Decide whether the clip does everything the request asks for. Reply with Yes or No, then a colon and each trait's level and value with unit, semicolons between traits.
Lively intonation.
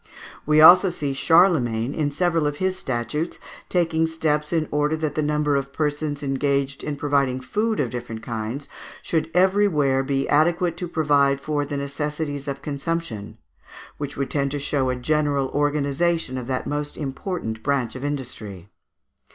No: narrow, 2.6 semitones